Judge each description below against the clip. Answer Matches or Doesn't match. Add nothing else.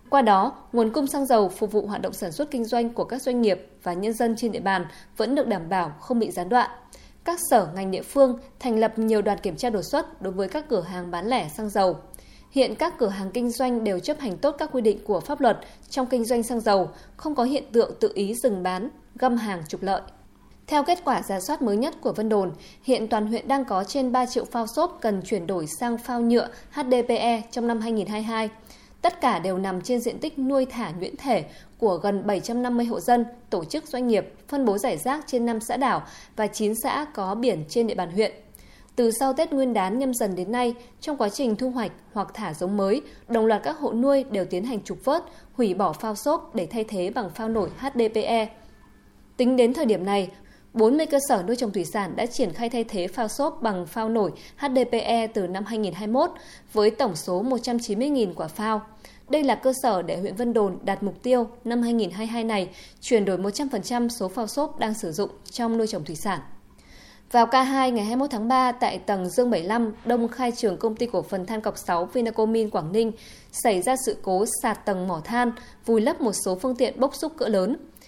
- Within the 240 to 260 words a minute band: Doesn't match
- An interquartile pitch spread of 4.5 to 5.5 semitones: Doesn't match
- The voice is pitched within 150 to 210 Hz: Doesn't match